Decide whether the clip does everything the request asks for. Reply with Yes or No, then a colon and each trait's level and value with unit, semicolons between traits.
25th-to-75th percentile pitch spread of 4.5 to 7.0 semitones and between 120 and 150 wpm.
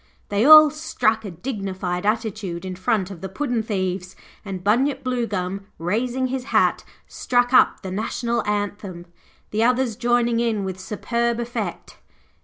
No: average, 4.1 semitones; average, 145 wpm